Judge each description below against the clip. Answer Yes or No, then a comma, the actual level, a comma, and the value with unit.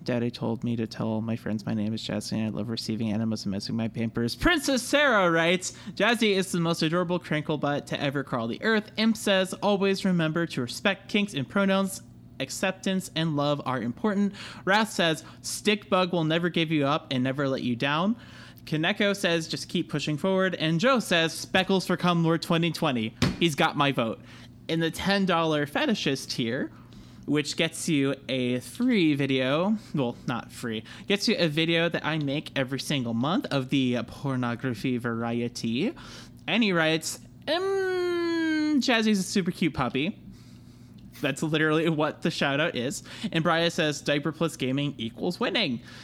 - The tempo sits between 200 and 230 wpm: No, average, 175 wpm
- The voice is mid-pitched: Yes, medium, 160 Hz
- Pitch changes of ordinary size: No, wide, 6.6 semitones